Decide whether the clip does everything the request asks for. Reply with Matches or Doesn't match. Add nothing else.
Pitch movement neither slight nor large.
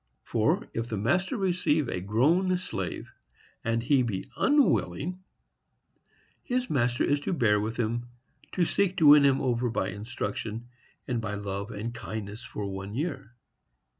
Doesn't match